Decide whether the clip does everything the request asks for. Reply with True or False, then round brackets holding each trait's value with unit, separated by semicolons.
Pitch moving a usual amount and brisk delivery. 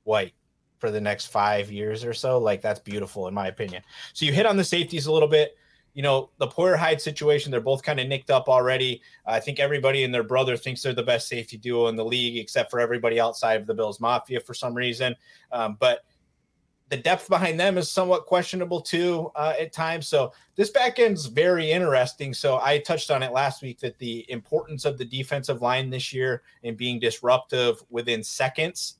True (4.6 semitones; 215 wpm)